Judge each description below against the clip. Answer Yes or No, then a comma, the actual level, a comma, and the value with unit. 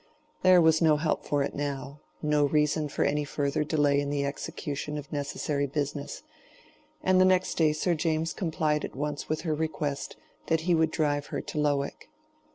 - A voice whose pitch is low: No, medium, 150 Hz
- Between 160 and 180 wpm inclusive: Yes, average, 175 wpm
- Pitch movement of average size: No, narrow, 1.8 semitones